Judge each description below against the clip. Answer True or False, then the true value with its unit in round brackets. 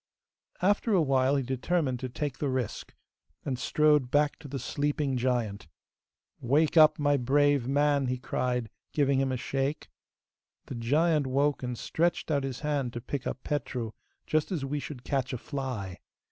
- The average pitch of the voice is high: False (135 Hz)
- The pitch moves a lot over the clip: False (2.6 semitones)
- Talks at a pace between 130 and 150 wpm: False (170 wpm)